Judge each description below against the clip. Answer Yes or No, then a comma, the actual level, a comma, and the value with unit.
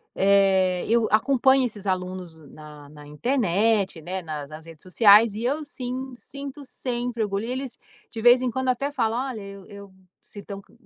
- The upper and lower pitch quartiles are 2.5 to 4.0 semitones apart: No, average, 5.2 semitones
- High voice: Yes, high, 215 Hz